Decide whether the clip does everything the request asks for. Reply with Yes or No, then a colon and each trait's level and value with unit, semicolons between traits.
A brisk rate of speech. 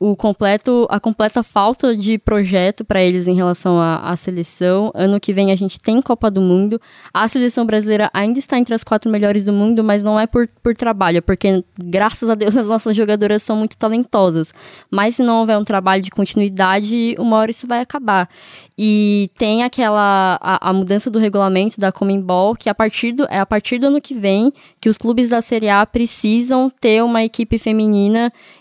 Yes: fast, 200 wpm